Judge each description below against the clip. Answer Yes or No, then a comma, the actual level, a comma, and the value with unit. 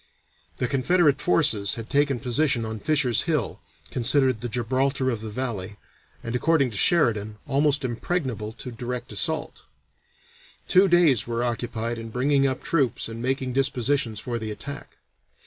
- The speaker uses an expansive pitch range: No, average, 3.8 semitones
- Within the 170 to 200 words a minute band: No, average, 150 wpm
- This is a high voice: No, low, 125 Hz